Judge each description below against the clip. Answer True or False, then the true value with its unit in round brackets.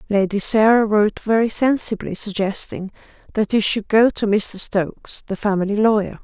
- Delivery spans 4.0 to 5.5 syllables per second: True (5.1 syllables/s)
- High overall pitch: True (210 Hz)